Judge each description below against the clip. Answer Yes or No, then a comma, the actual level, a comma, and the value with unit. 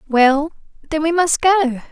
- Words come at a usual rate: Yes, average, 155 wpm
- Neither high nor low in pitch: No, very high, 300 Hz